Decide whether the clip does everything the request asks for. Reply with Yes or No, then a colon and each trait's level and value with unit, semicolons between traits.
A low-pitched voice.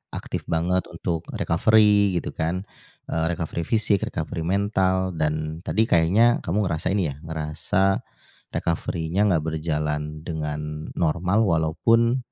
Yes: very low, 85 Hz